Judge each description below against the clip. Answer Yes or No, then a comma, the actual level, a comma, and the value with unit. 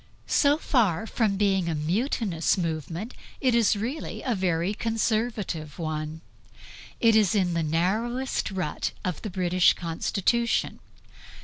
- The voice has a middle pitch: No, high, 195 Hz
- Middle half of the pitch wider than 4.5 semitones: Yes, average, 5.3 semitones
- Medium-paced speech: No, slow, 125 wpm